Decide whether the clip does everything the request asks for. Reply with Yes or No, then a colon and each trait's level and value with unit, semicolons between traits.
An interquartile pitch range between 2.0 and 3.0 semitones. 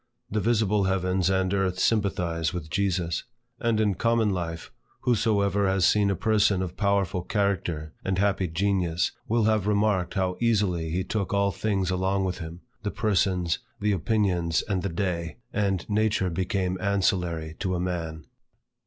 Yes: narrow, 2.4 semitones